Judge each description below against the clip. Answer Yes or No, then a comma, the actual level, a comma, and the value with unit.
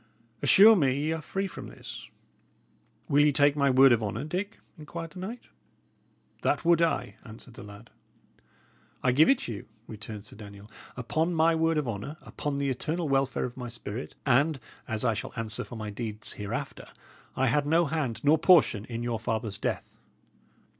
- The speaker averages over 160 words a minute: Yes, average, 180 wpm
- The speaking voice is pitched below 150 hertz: Yes, low, 135 Hz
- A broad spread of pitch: Yes, wide, 5.9 semitones